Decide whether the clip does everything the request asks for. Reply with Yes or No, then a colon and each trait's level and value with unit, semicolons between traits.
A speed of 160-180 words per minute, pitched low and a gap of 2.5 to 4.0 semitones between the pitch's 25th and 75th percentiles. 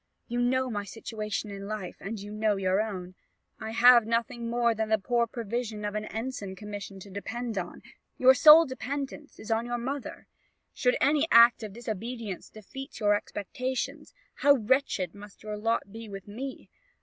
No: average, 175 wpm; high, 225 Hz; average, 3.0 semitones